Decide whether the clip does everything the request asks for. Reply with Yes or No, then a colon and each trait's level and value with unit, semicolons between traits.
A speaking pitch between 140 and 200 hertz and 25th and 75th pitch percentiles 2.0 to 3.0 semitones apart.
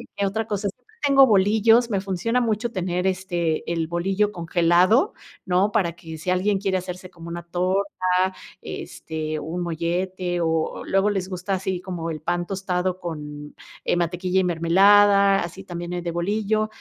Yes: medium, 185 Hz; narrow, 2.6 semitones